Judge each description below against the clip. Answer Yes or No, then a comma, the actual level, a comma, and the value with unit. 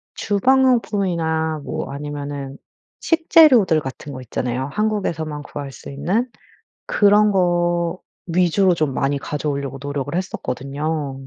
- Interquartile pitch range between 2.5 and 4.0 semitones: No, wide, 5.5 semitones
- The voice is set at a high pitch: No, medium, 160 Hz